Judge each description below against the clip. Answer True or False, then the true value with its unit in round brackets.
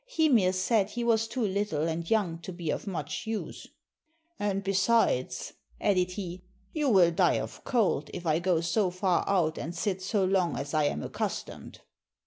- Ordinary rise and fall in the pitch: True (3.9 semitones)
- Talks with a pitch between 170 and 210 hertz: True (185 Hz)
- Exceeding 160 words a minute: True (175 wpm)